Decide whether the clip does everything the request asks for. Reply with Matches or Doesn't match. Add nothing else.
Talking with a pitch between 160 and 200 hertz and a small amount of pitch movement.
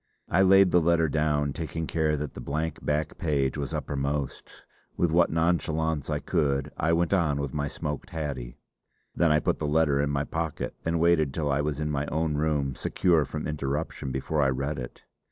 Doesn't match